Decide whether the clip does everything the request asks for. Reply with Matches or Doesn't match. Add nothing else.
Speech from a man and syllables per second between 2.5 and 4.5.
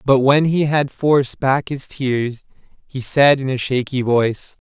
Matches